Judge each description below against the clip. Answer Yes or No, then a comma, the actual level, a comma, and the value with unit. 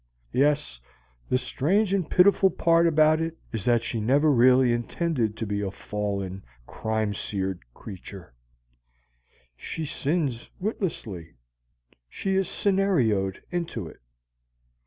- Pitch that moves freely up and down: Yes, wide, 8.2 semitones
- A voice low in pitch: Yes, low, 125 Hz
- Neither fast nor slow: No, slow, 115 wpm